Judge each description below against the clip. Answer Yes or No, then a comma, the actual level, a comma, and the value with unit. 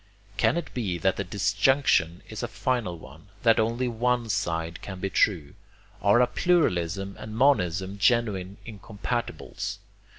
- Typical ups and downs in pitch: Yes, average, 4.6 semitones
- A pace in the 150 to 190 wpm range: No, average, 140 wpm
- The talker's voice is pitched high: No, low, 105 Hz